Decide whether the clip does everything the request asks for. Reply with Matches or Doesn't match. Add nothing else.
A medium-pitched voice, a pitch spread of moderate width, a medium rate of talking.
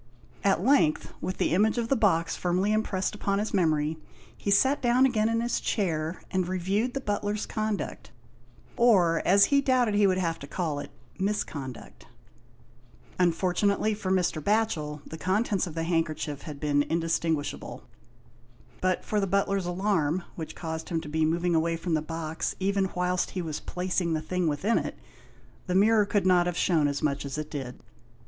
Matches